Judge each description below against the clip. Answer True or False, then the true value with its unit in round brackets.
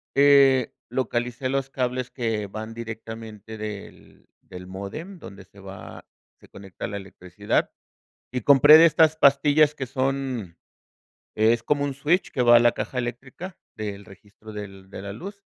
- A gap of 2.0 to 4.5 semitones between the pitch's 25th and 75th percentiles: False (5.0 semitones)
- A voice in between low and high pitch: False (120 Hz)